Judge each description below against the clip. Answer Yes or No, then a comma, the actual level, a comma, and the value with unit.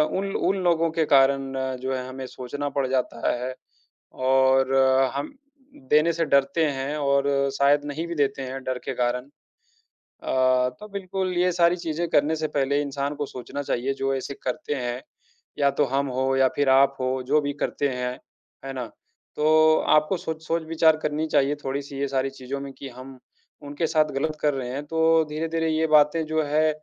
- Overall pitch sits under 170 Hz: Yes, medium, 140 Hz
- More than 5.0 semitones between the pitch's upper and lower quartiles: No, average, 2.9 semitones